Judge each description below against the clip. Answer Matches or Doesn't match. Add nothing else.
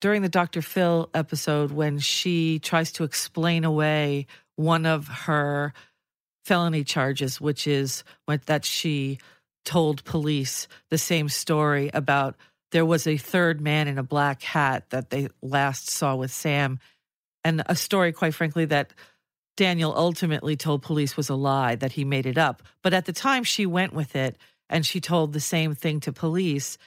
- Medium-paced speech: Matches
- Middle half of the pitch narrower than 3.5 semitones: Matches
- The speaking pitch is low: Doesn't match